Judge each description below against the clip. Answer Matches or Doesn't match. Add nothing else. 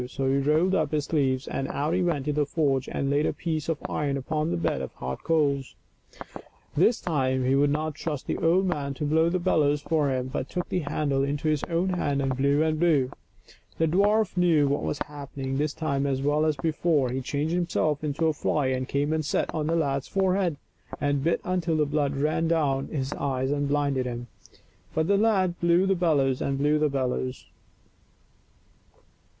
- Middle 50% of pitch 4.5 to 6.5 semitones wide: Doesn't match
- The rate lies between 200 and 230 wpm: Matches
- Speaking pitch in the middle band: Matches